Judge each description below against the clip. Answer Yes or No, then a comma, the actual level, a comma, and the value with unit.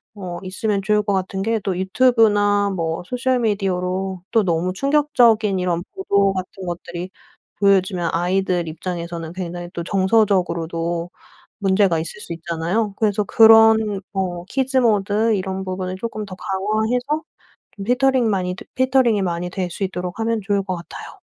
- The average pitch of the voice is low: No, high, 195 Hz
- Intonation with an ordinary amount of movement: Yes, average, 3.5 semitones